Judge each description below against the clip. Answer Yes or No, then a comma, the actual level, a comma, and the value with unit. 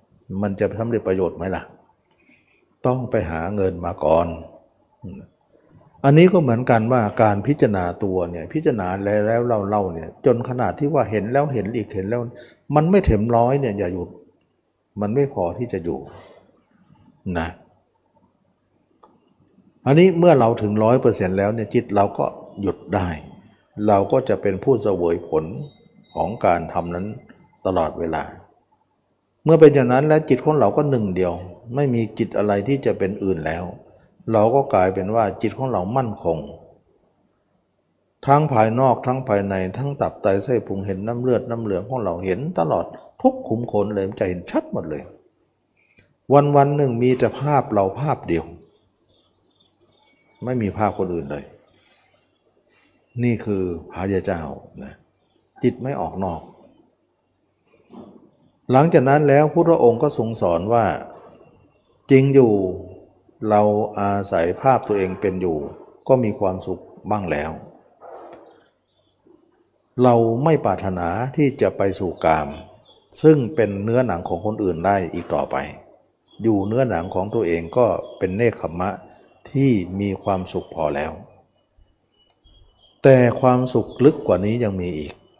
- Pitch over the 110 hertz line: No, low, 105 Hz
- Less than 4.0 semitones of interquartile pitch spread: No, average, 5.1 semitones